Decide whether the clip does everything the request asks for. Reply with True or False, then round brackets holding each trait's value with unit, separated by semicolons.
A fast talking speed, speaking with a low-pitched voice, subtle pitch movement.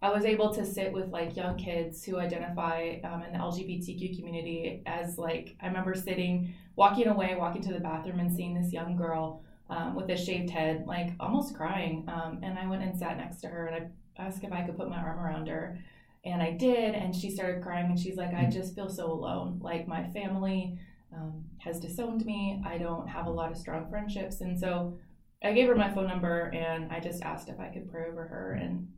False (225 wpm; 175 Hz; 2.2 semitones)